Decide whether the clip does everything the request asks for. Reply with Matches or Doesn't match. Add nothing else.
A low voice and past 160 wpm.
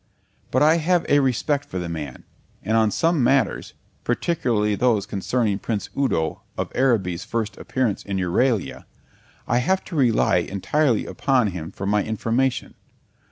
Doesn't match